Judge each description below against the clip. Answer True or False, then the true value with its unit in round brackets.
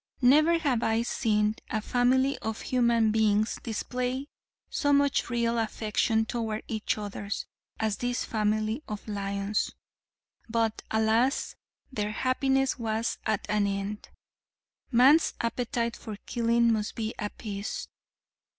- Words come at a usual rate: False (120 wpm)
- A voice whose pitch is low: False (225 Hz)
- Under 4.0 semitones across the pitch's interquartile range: True (2.5 semitones)